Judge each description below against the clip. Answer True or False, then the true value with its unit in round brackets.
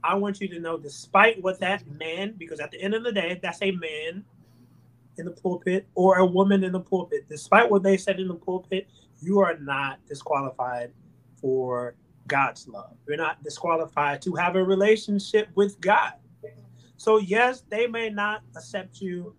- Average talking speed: True (180 wpm)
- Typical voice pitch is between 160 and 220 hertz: True (185 Hz)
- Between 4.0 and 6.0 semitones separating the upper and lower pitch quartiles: True (5.2 semitones)